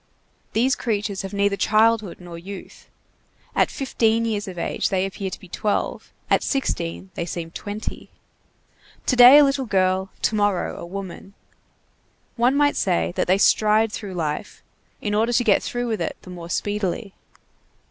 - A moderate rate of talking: Yes, average, 165 wpm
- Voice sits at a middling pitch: No, high, 205 Hz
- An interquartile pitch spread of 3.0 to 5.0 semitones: Yes, average, 3.4 semitones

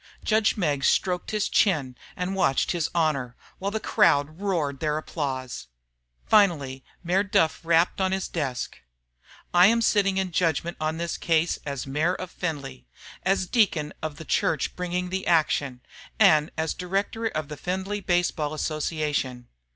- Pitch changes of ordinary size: Yes, average, 4.1 semitones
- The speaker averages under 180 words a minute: Yes, average, 160 wpm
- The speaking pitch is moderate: Yes, medium, 165 Hz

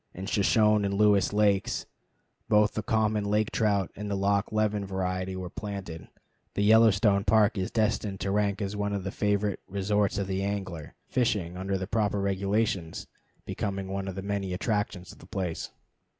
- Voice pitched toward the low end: Yes, low, 100 Hz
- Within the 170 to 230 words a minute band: Yes, average, 175 wpm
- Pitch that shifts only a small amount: Yes, narrow, 1.5 semitones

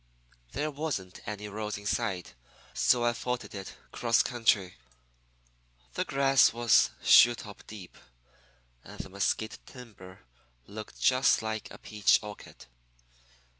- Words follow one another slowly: Yes, slow, 125 wpm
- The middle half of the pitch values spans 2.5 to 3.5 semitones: Yes, average, 3.1 semitones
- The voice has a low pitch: Yes, low, 110 Hz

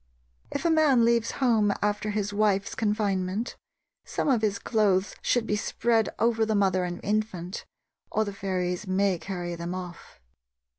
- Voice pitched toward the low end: No, high, 205 Hz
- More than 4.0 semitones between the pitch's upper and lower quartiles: No, average, 2.9 semitones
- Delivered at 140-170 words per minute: Yes, average, 155 wpm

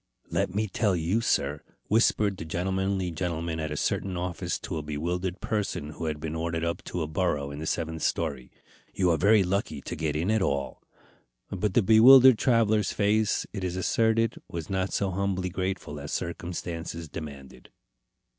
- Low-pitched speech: Yes, very low, 90 Hz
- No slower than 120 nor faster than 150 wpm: No, average, 175 wpm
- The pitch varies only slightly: No, average, 4.0 semitones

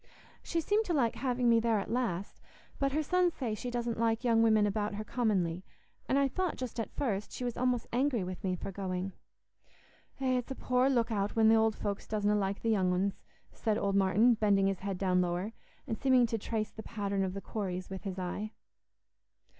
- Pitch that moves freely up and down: No, average, 3.9 semitones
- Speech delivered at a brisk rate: Yes, fast, 215 wpm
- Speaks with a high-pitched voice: Yes, high, 220 Hz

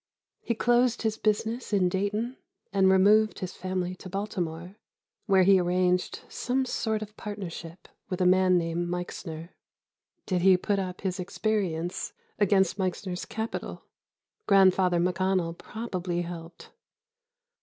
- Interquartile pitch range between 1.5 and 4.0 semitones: Yes, average, 2.7 semitones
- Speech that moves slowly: Yes, slow, 125 wpm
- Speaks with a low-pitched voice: No, medium, 185 Hz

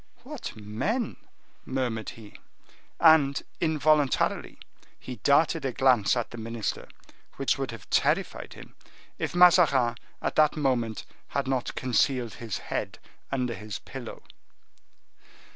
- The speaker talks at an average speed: No, slow, 120 wpm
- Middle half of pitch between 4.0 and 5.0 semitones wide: Yes, average, 4.6 semitones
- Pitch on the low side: Yes, low, 130 Hz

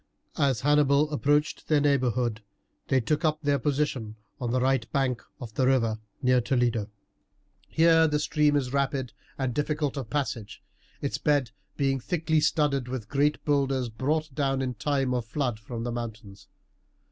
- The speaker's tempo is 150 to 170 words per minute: Yes, average, 160 wpm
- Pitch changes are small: No, average, 3.2 semitones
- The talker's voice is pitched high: No, low, 135 Hz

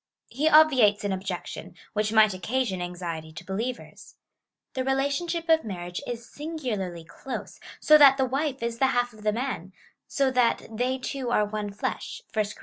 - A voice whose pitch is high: Yes, high, 235 Hz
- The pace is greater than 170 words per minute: Yes, average, 180 wpm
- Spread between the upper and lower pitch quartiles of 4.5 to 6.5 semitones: Yes, average, 5.1 semitones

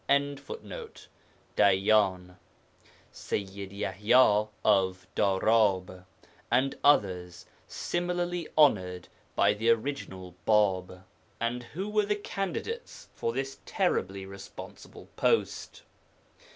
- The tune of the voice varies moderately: No, wide, 7.0 semitones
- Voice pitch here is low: Yes, low, 105 Hz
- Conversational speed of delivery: No, slow, 85 wpm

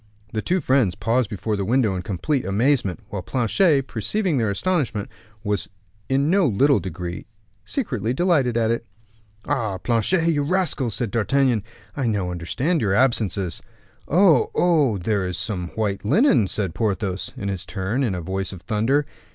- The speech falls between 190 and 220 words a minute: No, average, 160 wpm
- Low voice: Yes, low, 115 Hz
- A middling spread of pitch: No, wide, 6.0 semitones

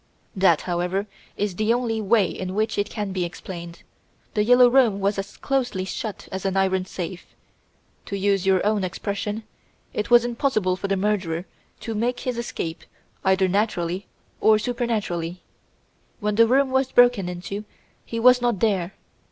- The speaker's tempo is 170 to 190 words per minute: No, average, 160 wpm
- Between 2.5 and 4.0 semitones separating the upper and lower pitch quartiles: Yes, average, 3.6 semitones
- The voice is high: Yes, high, 200 Hz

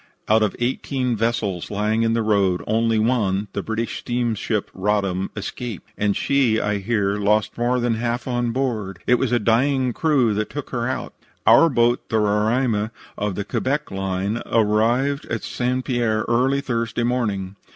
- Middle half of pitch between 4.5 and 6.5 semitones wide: No, average, 2.8 semitones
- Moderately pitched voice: No, low, 115 Hz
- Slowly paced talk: No, average, 165 wpm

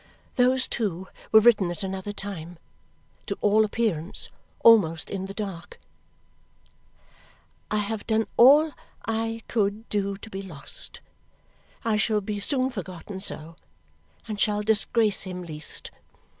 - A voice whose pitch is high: Yes, high, 205 Hz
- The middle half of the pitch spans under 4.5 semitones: Yes, average, 2.8 semitones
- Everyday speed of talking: No, slow, 130 wpm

